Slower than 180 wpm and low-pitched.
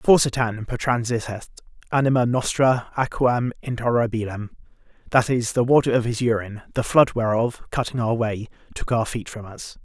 Yes: average, 145 wpm; low, 120 Hz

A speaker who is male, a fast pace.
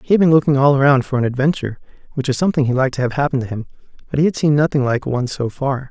Yes: male; fast, 285 wpm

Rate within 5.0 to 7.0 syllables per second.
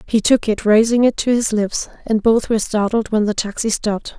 Yes: 5.4 syllables/s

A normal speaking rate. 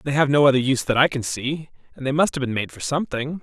No: fast, 300 wpm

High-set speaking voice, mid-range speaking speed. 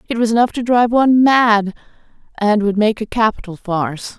Yes: high, 220 Hz; average, 185 wpm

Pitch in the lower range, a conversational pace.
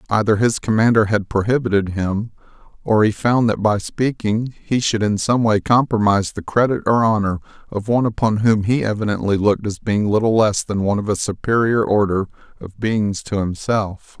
Yes: low, 105 Hz; average, 180 wpm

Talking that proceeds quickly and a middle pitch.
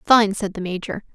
No: fast, 210 wpm; high, 200 Hz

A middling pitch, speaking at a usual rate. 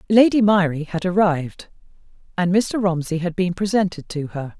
Yes: medium, 180 Hz; average, 155 wpm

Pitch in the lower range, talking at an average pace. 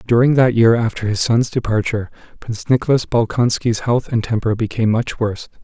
Yes: low, 115 Hz; average, 170 wpm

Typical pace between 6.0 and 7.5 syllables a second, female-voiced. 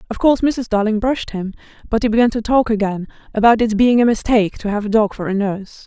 Yes: 6.5 syllables/s; female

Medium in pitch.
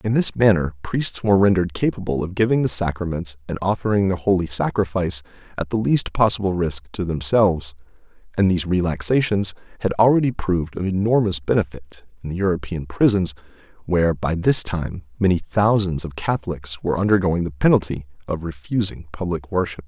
No: very low, 90 Hz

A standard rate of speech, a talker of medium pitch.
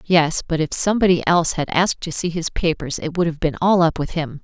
No: fast, 255 wpm; medium, 165 Hz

